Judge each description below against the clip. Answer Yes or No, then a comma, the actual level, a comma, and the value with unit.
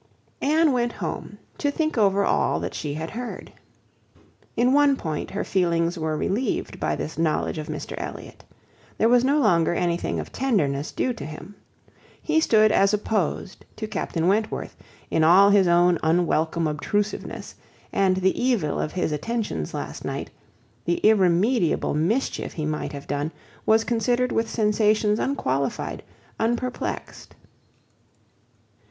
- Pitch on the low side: No, high, 195 Hz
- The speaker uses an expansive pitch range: Yes, wide, 6.1 semitones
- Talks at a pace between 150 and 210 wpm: No, average, 140 wpm